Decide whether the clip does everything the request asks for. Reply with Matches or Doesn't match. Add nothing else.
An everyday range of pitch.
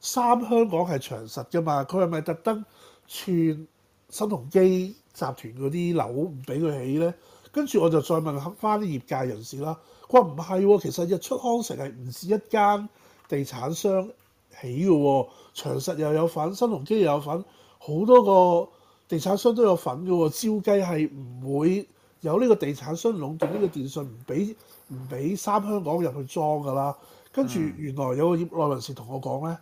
Doesn't match